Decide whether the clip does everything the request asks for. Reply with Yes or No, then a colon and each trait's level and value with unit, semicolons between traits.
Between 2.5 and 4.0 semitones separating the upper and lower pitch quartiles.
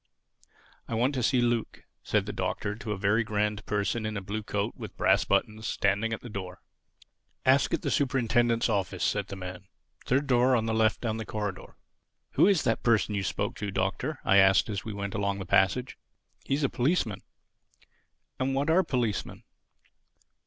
Yes: average, 3.6 semitones